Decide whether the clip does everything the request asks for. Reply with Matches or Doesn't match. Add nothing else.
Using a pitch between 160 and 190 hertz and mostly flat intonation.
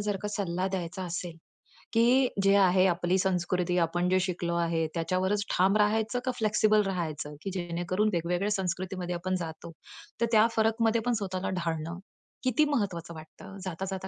Doesn't match